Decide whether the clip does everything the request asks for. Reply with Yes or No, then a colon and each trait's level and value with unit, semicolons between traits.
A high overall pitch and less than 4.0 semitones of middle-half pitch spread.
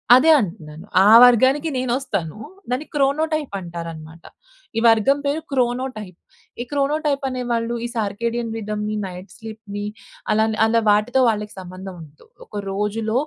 No: high, 225 Hz; average, 4.3 semitones